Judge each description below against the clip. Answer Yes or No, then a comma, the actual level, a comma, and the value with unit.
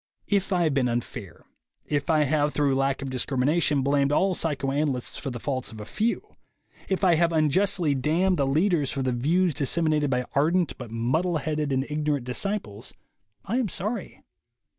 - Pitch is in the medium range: Yes, medium, 150 Hz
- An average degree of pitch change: Yes, average, 4.2 semitones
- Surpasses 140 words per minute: Yes, average, 180 wpm